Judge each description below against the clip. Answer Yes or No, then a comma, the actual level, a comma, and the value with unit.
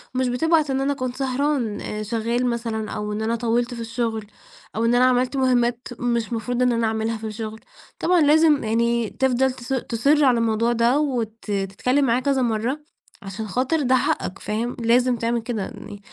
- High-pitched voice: Yes, high, 240 Hz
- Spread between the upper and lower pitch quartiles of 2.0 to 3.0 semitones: Yes, narrow, 2.5 semitones